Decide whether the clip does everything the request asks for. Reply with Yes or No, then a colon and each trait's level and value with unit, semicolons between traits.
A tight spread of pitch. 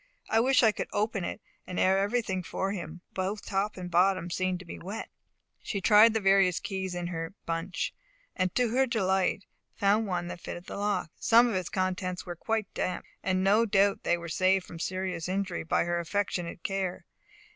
Yes: narrow, 2.3 semitones